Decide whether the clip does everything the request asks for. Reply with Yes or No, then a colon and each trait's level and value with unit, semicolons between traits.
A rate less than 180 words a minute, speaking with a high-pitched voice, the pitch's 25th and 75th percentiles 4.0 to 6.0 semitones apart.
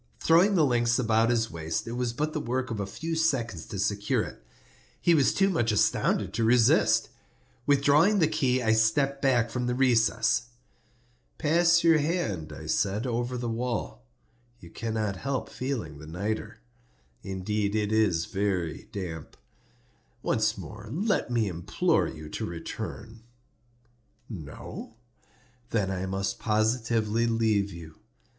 No: average, 145 wpm; low, 115 Hz; average, 4.6 semitones